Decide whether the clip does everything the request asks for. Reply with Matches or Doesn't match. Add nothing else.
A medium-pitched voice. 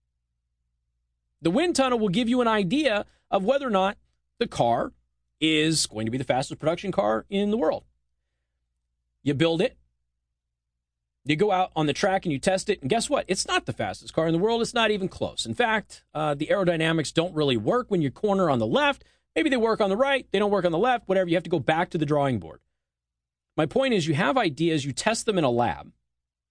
Matches